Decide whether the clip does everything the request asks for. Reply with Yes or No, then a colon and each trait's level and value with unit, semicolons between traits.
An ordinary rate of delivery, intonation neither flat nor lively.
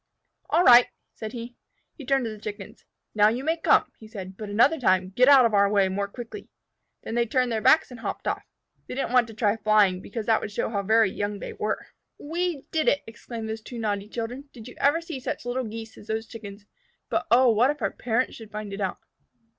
No: fast, 235 wpm; average, 3.2 semitones